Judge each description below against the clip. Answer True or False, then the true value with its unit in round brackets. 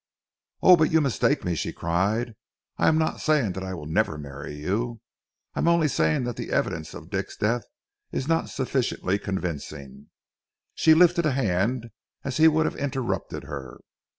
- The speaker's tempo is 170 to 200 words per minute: True (175 wpm)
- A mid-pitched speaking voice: False (115 Hz)